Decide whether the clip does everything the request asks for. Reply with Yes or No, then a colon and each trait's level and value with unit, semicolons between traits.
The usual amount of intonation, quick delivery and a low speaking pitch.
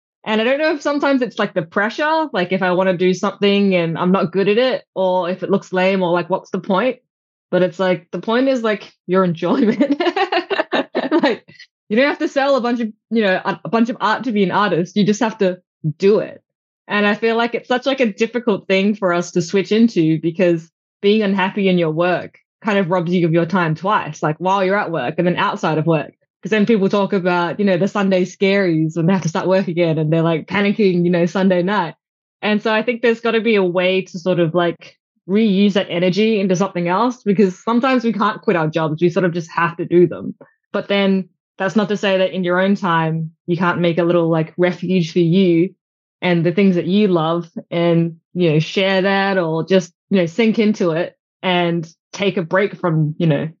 No: average, 3.1 semitones; fast, 235 wpm; high, 190 Hz